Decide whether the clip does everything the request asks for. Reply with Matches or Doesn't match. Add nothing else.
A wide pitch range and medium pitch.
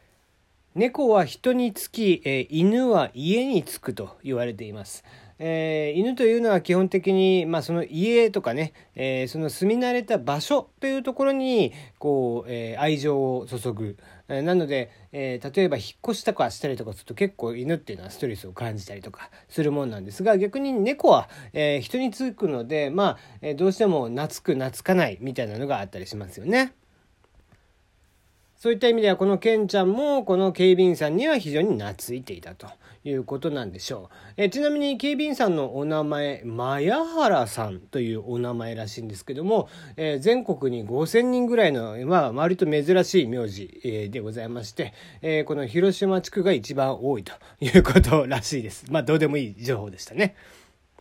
Matches